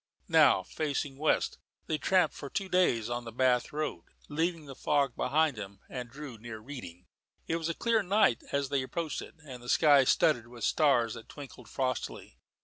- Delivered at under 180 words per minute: No, average, 185 wpm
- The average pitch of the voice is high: No, medium, 140 Hz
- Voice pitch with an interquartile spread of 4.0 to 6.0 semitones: Yes, average, 4.3 semitones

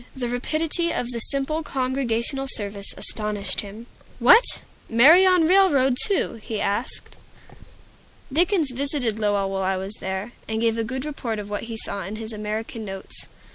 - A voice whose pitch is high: Yes, high, 235 Hz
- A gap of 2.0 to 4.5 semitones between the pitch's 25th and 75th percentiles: No, average, 5.0 semitones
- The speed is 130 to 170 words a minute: Yes, average, 160 wpm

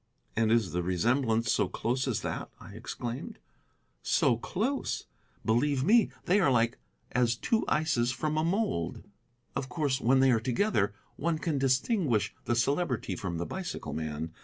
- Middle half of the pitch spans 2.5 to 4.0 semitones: No, wide, 5.5 semitones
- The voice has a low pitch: Yes, low, 125 Hz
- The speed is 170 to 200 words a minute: No, average, 160 wpm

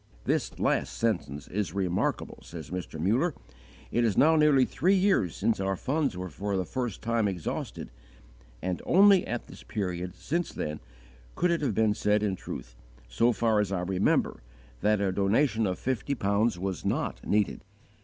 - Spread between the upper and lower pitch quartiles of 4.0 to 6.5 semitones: Yes, average, 5.3 semitones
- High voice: No, low, 105 Hz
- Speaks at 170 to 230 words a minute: Yes, average, 175 wpm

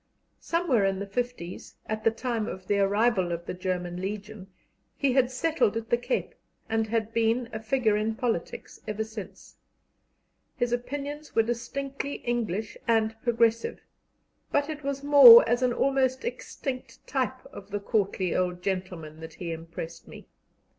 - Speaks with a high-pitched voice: Yes, high, 225 Hz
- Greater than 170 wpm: No, average, 155 wpm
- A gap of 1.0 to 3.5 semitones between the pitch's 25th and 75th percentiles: No, average, 4.4 semitones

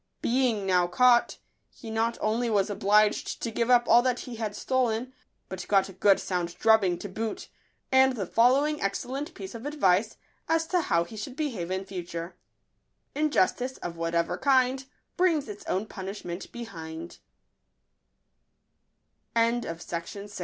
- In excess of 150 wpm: No, average, 140 wpm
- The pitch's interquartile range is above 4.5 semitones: Yes, average, 5.1 semitones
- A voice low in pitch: No, high, 220 Hz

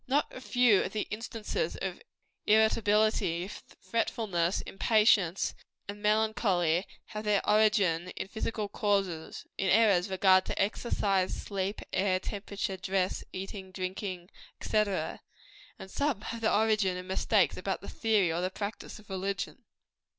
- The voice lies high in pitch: Yes, high, 200 Hz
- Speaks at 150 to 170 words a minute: No, slow, 135 wpm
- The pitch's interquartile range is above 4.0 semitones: No, narrow, 2.5 semitones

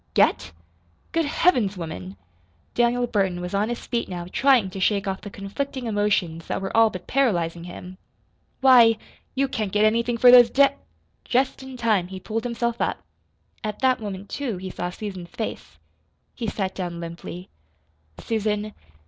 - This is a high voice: Yes, high, 210 Hz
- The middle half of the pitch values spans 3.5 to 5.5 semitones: Yes, average, 4.4 semitones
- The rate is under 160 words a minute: No, average, 165 wpm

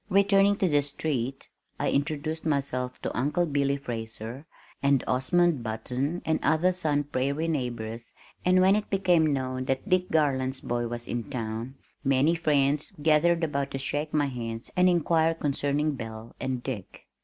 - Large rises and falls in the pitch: No, average, 4.1 semitones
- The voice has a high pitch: No, medium, 140 Hz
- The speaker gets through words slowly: No, average, 155 wpm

